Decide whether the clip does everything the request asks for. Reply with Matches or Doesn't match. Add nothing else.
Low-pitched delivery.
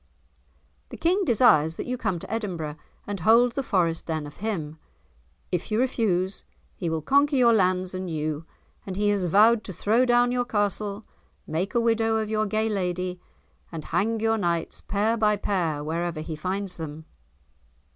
Doesn't match